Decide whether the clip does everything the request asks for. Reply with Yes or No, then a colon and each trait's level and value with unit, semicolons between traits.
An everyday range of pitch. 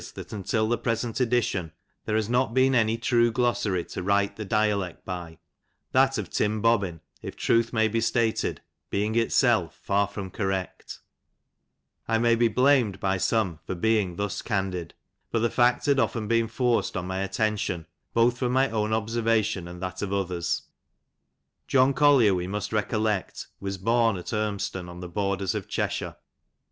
Yes: average, 3.3 semitones